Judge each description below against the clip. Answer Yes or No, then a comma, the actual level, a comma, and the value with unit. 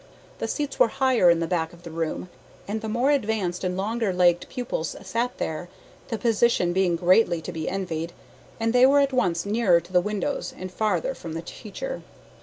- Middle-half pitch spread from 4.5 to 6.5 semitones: Yes, average, 5.2 semitones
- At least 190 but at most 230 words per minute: Yes, average, 200 wpm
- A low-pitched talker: No, high, 190 Hz